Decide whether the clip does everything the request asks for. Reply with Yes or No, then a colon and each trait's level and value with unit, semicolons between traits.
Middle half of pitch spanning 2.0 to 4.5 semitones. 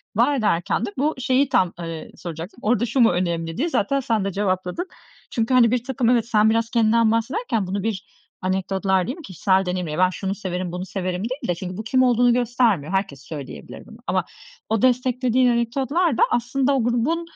No: average, 5.1 semitones